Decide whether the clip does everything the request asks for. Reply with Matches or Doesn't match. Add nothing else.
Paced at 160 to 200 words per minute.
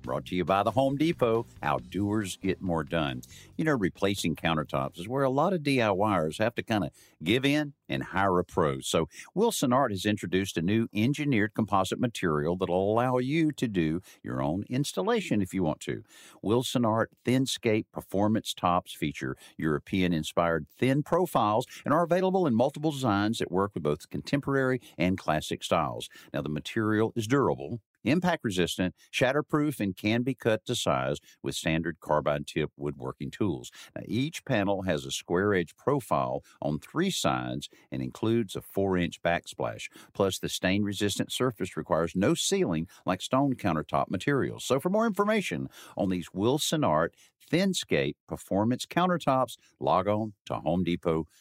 Matches